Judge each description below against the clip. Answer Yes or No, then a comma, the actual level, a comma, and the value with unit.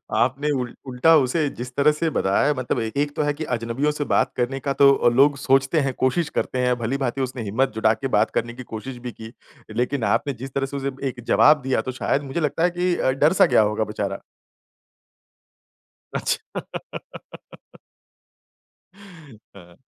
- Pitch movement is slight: No, average, 3.0 semitones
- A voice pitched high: No, low, 135 Hz